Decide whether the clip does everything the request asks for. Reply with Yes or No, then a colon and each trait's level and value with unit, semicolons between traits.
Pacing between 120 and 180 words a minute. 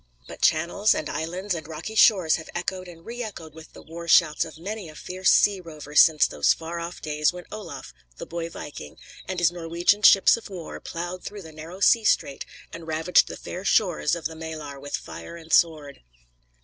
No: average, 200 wpm